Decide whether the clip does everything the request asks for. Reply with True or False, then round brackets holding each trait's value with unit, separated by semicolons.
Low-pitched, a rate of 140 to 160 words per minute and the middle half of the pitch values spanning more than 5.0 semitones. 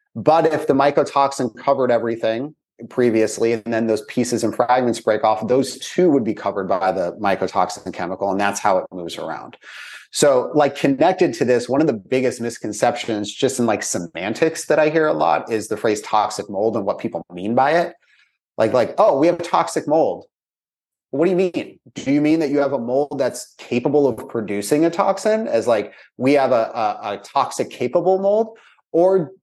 False (130 Hz; 200 wpm; 5.5 semitones)